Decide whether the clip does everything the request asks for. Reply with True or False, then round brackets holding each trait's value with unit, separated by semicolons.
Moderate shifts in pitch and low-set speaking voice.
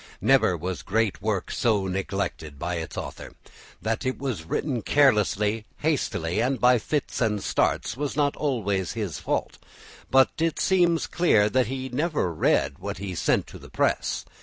False (5.9 semitones; 110 Hz)